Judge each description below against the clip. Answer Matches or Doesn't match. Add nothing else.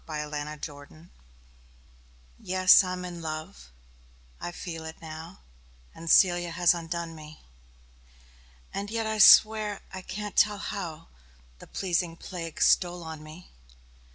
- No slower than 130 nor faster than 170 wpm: Matches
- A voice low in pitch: Doesn't match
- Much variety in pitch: Doesn't match